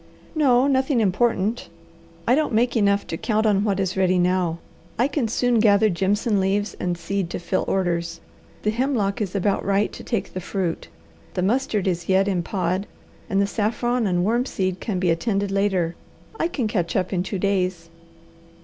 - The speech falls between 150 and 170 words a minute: No, average, 180 wpm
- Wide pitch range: No, average, 3.5 semitones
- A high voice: Yes, high, 200 Hz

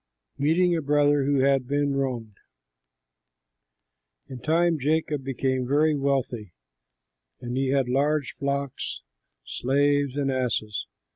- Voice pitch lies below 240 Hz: Yes, medium, 140 Hz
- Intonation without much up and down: Yes, narrow, 1.9 semitones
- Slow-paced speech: Yes, slow, 115 wpm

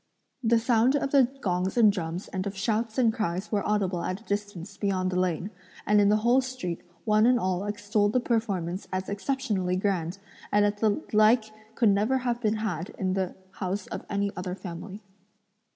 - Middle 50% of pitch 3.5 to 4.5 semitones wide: No, average, 3.1 semitones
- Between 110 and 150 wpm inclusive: No, average, 190 wpm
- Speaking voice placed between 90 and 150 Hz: No, high, 205 Hz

